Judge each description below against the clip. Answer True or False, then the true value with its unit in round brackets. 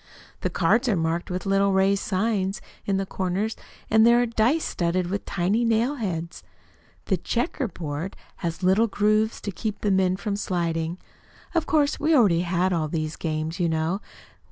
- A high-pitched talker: True (195 Hz)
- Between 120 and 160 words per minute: False (170 wpm)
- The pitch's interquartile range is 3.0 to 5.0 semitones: True (4.1 semitones)